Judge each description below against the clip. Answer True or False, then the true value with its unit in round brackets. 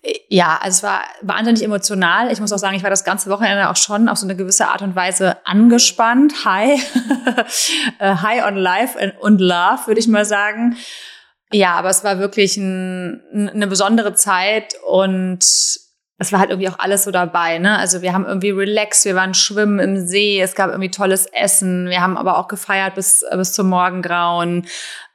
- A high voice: True (200 Hz)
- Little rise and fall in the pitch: True (2.3 semitones)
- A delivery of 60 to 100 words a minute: False (185 wpm)